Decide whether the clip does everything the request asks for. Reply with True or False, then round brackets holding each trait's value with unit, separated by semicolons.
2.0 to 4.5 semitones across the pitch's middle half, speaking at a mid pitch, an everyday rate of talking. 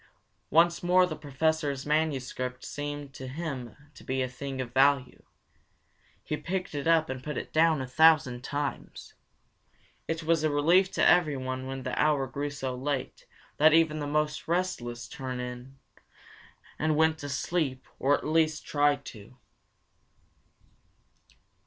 True (3.2 semitones; 145 Hz; 145 wpm)